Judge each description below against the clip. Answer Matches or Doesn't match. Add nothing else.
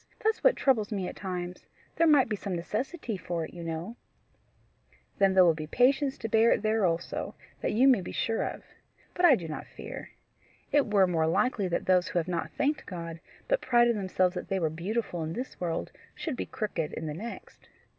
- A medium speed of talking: Doesn't match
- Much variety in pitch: Matches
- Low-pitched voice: Doesn't match